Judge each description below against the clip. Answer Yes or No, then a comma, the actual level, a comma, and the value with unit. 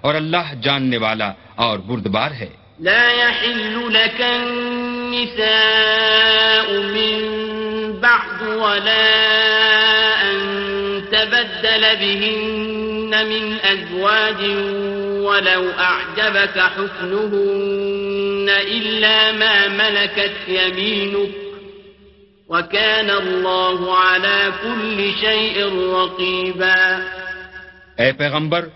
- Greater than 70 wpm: No, slow, 65 wpm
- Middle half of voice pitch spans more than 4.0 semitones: No, average, 2.7 semitones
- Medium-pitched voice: No, high, 200 Hz